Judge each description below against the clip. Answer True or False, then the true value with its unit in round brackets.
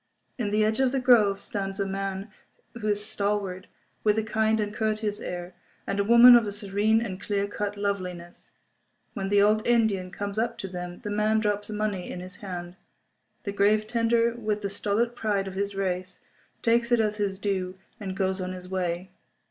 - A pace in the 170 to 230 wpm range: True (190 wpm)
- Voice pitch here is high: True (205 Hz)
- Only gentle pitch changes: True (2.1 semitones)